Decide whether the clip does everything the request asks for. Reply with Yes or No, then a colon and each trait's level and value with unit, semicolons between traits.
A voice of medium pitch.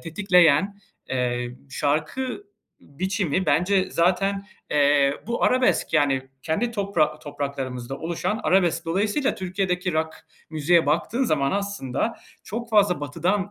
Yes: medium, 175 Hz